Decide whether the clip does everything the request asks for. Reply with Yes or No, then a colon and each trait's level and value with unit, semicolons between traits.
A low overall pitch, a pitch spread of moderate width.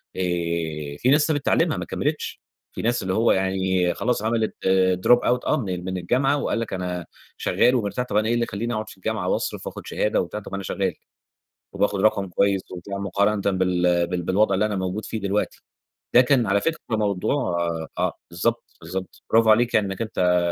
Yes: low, 100 Hz; average, 3.9 semitones